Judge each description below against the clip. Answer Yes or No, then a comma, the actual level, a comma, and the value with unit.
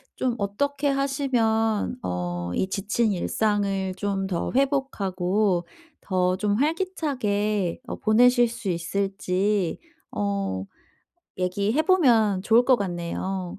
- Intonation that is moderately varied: Yes, average, 4.6 semitones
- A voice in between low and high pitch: No, high, 205 Hz